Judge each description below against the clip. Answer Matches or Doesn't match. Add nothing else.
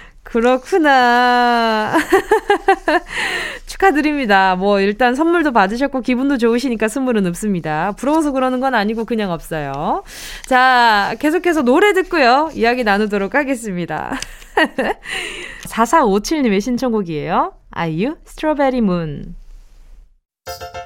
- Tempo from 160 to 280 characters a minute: Matches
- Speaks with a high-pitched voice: Matches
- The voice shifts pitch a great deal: Matches